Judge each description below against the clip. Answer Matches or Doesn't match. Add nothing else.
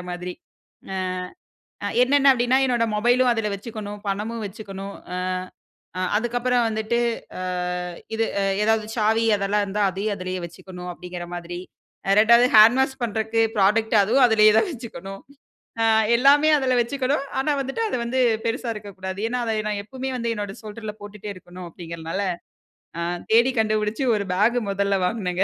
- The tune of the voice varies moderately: Matches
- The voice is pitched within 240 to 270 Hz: Doesn't match